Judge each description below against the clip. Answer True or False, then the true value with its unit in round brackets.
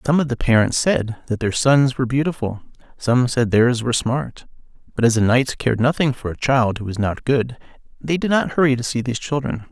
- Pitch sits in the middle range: False (125 Hz)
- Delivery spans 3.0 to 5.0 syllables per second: False (5.6 syllables/s)